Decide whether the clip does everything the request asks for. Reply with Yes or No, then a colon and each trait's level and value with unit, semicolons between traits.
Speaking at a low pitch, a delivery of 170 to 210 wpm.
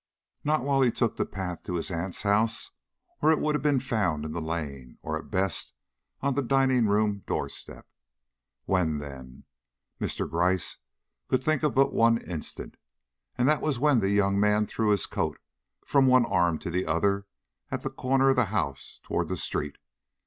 Yes: low, 105 Hz; average, 185 wpm